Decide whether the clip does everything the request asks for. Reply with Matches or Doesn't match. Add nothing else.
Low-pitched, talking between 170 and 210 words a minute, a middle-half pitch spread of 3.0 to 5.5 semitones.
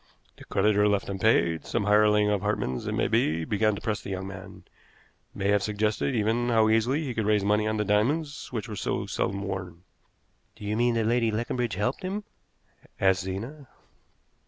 Doesn't match